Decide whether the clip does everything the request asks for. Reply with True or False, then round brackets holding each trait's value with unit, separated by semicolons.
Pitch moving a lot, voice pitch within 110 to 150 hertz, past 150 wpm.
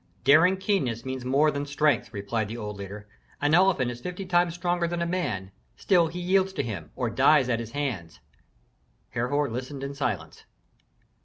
True (6.9 semitones; 140 Hz; 175 wpm)